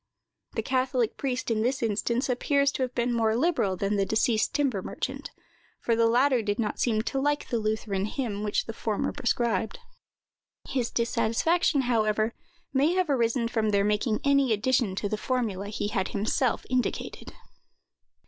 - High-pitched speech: Yes, high, 230 Hz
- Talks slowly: No, average, 165 wpm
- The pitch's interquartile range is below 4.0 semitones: Yes, average, 3.3 semitones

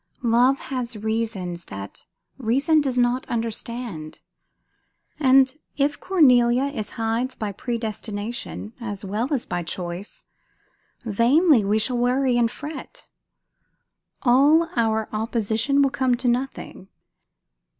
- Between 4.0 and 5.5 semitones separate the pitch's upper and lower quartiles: No, average, 3.3 semitones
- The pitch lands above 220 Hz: Yes, high, 240 Hz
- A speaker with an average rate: No, slow, 110 wpm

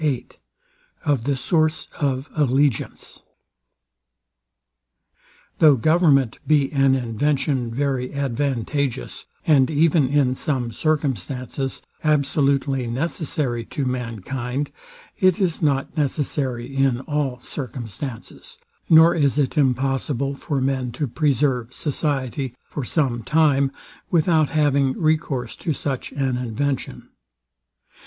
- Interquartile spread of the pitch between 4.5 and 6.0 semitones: No, average, 2.8 semitones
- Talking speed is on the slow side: Yes, slow, 105 wpm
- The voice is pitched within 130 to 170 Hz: Yes, low, 135 Hz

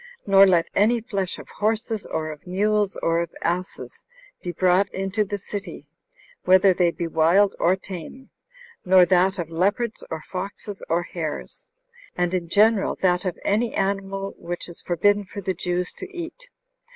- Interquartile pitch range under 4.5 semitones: Yes, narrow, 2.6 semitones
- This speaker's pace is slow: No, average, 165 wpm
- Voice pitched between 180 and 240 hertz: Yes, high, 190 Hz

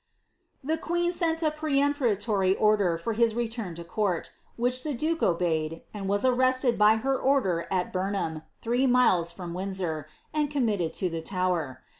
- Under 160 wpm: No, average, 165 wpm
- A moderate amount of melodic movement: No, wide, 6.6 semitones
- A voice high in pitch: Yes, high, 215 Hz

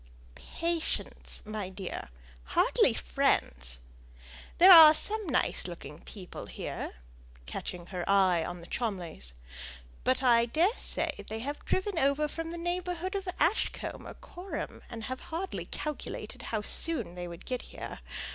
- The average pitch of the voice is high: Yes, very high, 255 Hz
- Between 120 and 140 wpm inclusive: Yes, slow, 135 wpm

